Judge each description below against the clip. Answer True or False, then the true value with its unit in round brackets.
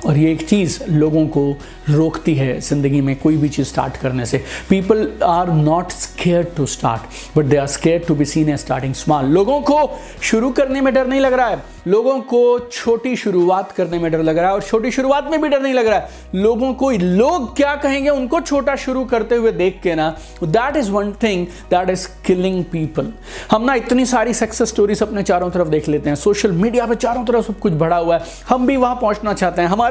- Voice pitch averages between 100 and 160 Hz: False (190 Hz)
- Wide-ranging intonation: True (7.4 semitones)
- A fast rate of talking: True (225 wpm)